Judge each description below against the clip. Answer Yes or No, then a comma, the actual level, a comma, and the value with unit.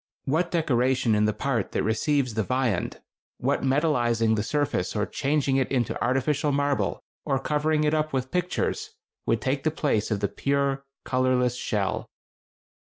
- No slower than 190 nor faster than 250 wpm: No, average, 160 wpm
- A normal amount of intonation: Yes, average, 4.0 semitones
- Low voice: Yes, low, 130 Hz